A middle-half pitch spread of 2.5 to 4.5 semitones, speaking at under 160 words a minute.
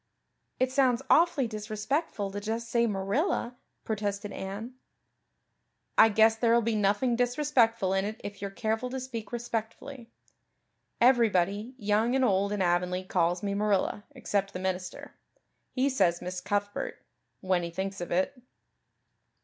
Yes: average, 3.6 semitones; average, 140 wpm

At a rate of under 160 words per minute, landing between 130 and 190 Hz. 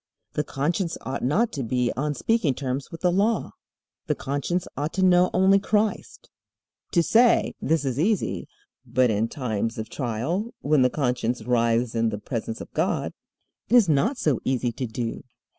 No: average, 175 wpm; medium, 140 Hz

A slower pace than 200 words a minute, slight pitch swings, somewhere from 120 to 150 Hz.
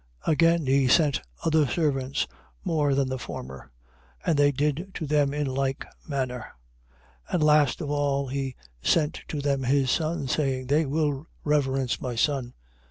Yes: average, 165 wpm; narrow, 2.2 semitones; medium, 140 Hz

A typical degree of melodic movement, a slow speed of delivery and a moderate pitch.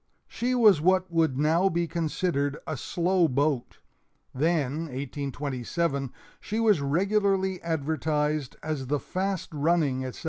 Yes: average, 4.5 semitones; slow, 125 wpm; medium, 155 Hz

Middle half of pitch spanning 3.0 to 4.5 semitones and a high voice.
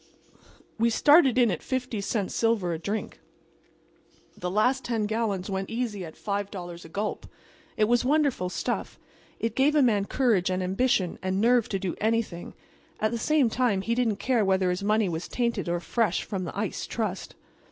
Yes: average, 3.9 semitones; high, 215 Hz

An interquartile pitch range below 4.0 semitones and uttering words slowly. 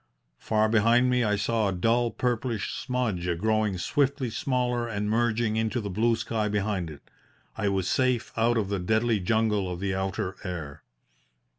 No: average, 3.2 semitones; average, 165 wpm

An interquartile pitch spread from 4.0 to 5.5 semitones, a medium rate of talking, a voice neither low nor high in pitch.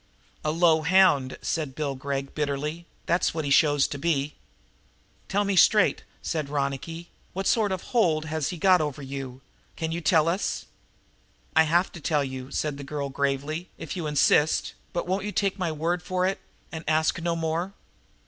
No: average, 3.5 semitones; average, 185 wpm; medium, 160 Hz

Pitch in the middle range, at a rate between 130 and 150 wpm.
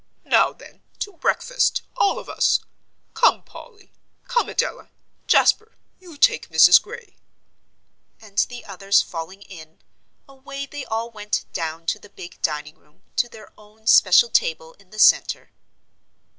No: high, 210 Hz; average, 145 wpm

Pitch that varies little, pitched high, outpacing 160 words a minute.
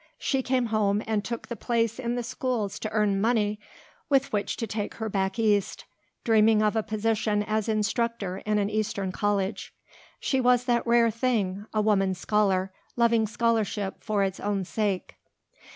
Yes: narrow, 2.3 semitones; high, 215 Hz; average, 170 wpm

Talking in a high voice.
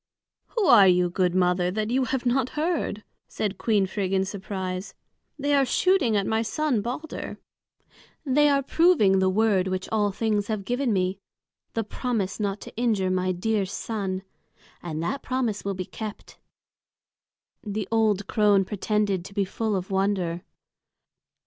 Yes: high, 205 Hz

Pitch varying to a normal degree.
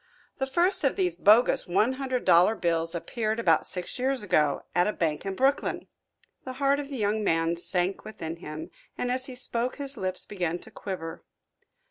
No: wide, 7.0 semitones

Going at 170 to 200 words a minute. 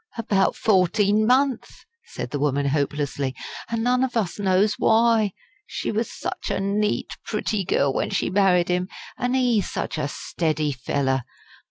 No: average, 155 wpm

